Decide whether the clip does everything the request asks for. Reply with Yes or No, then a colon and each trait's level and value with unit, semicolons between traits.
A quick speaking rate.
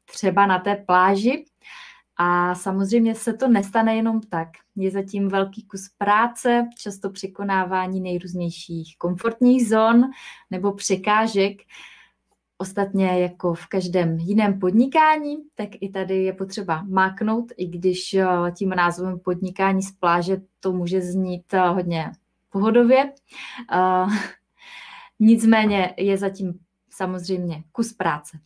No: slow, 115 wpm